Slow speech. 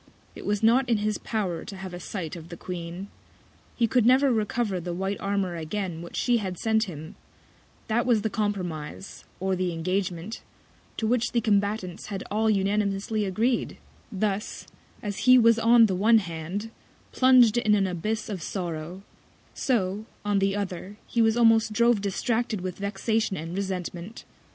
No: average, 165 wpm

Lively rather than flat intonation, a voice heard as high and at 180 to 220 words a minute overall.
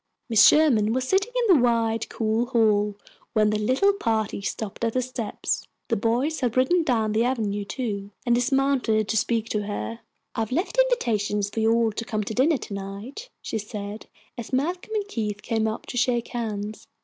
No: average, 3.4 semitones; high, 230 Hz; average, 195 wpm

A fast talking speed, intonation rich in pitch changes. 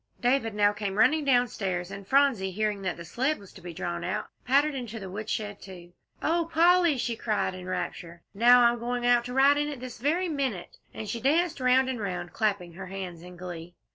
Yes: fast, 210 wpm; wide, 6.0 semitones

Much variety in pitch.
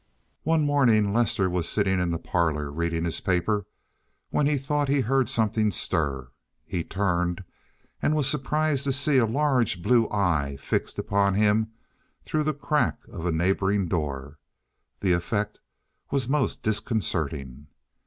Yes: wide, 7.5 semitones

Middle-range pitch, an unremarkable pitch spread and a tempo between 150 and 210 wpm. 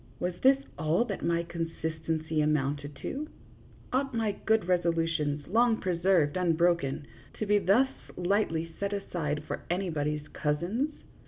No: medium, 170 Hz; average, 4.7 semitones; slow, 135 wpm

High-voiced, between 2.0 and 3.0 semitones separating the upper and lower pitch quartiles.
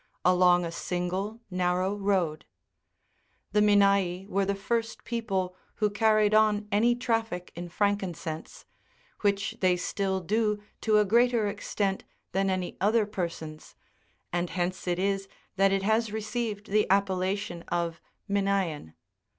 Yes: high, 195 Hz; narrow, 2.6 semitones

